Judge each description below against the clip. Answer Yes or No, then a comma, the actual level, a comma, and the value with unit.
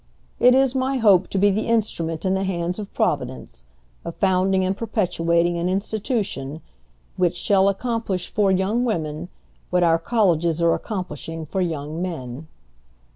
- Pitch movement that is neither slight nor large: Yes, average, 3.8 semitones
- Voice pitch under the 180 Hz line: No, medium, 185 Hz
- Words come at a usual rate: Yes, average, 150 wpm